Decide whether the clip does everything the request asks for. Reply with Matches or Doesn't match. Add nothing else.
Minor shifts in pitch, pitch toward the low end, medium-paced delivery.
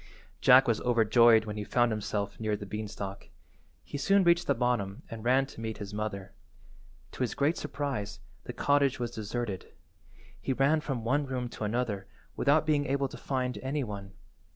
Doesn't match